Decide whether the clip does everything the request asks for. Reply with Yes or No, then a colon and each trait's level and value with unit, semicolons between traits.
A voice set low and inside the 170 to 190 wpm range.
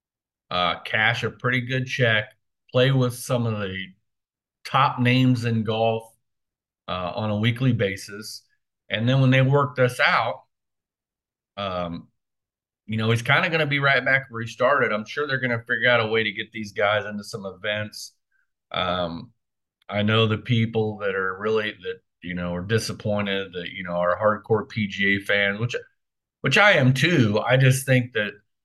Yes: low, 110 Hz; average, 180 wpm